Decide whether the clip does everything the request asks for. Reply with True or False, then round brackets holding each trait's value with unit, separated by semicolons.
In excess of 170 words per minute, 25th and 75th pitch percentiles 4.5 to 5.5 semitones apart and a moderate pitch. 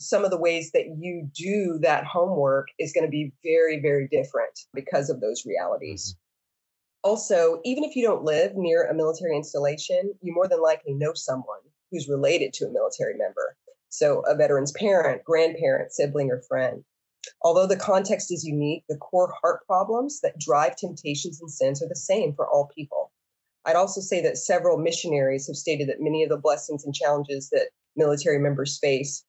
True (180 wpm; 4.8 semitones; 165 Hz)